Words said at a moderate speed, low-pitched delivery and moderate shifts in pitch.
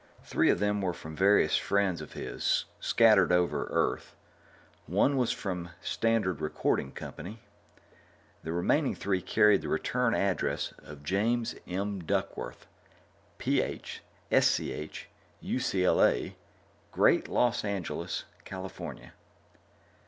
No: slow, 110 wpm; very low, 95 Hz; average, 3.1 semitones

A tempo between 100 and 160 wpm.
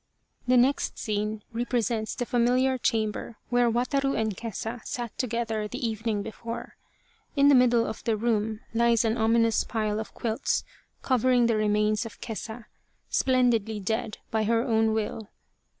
Yes: average, 150 wpm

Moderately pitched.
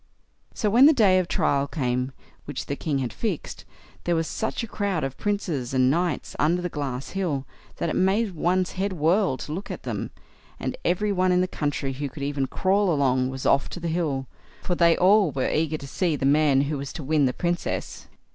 Yes: medium, 160 Hz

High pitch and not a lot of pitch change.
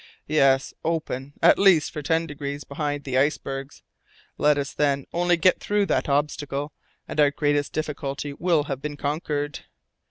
No: medium, 145 Hz; narrow, 1.8 semitones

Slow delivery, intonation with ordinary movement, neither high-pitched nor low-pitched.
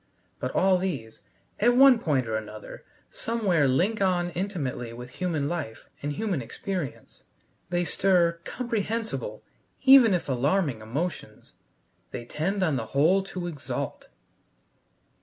No: slow, 125 wpm; wide, 6.5 semitones; medium, 175 Hz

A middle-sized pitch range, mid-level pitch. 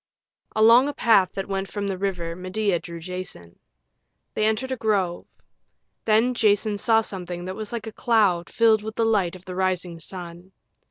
No: average, 3.3 semitones; high, 195 Hz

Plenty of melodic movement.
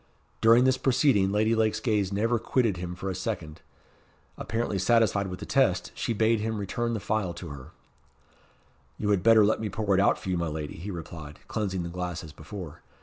No: average, 4.0 semitones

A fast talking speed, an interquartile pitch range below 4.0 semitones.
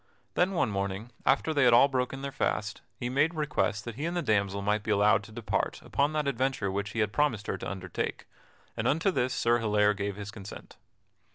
No: fast, 215 wpm; average, 5.2 semitones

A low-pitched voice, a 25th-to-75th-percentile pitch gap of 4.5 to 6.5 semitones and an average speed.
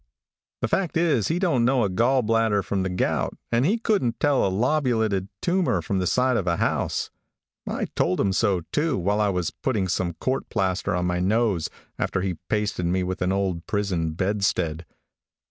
Yes: low, 100 Hz; wide, 5.4 semitones; average, 190 wpm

